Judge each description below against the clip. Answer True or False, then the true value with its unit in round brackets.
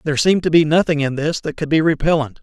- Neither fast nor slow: False (275 wpm)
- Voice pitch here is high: False (155 Hz)